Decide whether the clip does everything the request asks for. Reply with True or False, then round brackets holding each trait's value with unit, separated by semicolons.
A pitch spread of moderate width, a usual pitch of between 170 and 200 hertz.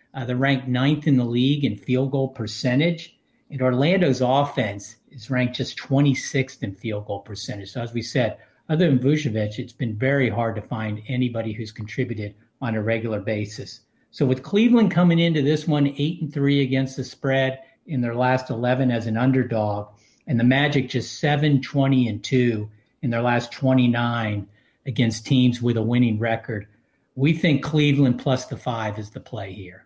False (3.3 semitones; 125 Hz)